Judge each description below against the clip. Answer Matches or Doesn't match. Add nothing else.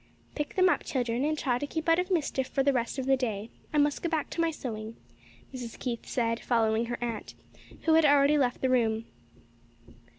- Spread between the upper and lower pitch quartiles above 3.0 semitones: Matches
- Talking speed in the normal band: Doesn't match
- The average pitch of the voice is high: Matches